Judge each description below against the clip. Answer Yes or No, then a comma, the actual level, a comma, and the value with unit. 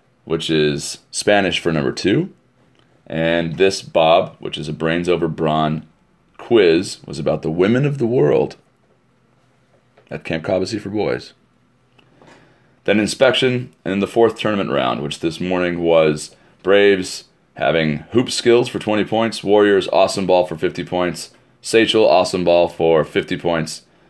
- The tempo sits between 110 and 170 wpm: Yes, average, 145 wpm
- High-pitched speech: No, very low, 90 Hz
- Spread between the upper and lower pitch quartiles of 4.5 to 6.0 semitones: Yes, wide, 5.5 semitones